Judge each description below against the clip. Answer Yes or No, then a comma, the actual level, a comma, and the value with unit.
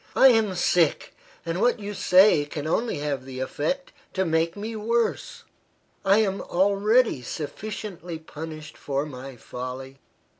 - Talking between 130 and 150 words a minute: Yes, average, 140 wpm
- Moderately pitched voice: Yes, medium, 170 Hz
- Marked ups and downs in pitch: Yes, wide, 6.3 semitones